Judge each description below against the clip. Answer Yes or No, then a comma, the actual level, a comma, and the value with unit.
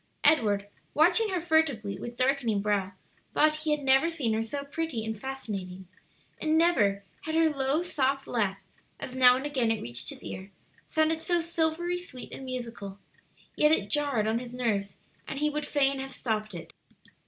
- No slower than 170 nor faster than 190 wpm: Yes, average, 175 wpm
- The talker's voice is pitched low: No, very high, 265 Hz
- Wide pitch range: Yes, wide, 6.1 semitones